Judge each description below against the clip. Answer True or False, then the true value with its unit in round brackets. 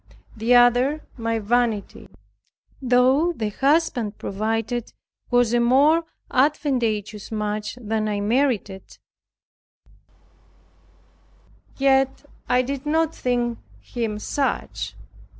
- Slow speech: True (90 wpm)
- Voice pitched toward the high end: True (245 Hz)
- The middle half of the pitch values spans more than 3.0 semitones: True (3.6 semitones)